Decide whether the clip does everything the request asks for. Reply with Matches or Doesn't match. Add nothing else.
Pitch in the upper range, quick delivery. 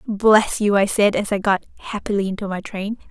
Matches